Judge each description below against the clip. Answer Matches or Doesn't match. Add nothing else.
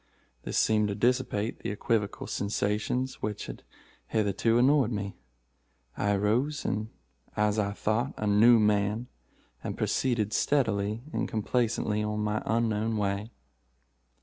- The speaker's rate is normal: Doesn't match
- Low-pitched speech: Matches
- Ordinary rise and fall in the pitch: Doesn't match